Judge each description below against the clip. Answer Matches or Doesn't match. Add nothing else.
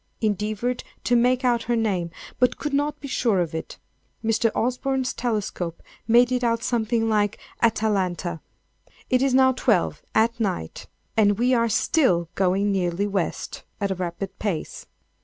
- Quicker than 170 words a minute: Doesn't match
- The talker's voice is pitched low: Doesn't match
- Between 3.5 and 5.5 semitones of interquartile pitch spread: Matches